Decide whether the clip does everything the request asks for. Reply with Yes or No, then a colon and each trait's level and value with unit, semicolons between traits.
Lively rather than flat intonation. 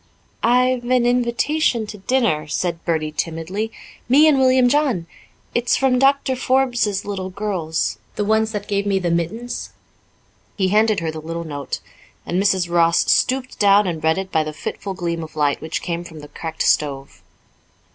Yes: wide, 6.5 semitones